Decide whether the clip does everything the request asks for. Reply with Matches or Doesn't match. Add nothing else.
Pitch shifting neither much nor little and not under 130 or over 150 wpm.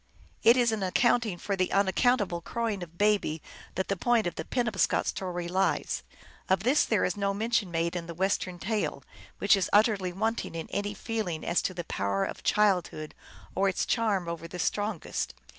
Doesn't match